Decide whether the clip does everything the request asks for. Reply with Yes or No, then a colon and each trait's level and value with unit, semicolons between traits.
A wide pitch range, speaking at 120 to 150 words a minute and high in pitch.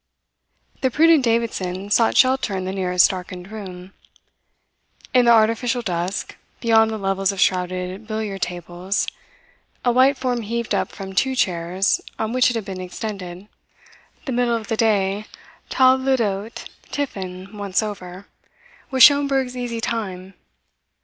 No: average, 4.2 semitones; average, 140 wpm; high, 210 Hz